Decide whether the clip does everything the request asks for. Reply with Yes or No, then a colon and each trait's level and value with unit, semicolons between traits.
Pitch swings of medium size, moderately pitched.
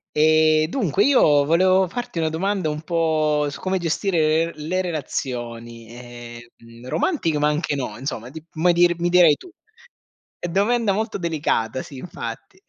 Yes: average, 4.2 semitones; medium, 160 Hz